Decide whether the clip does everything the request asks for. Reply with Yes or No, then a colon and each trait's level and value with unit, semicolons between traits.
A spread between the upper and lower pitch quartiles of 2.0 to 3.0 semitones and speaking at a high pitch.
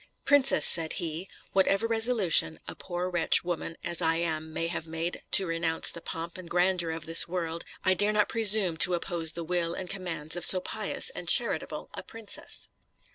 No: narrow, 2.5 semitones; medium, 175 Hz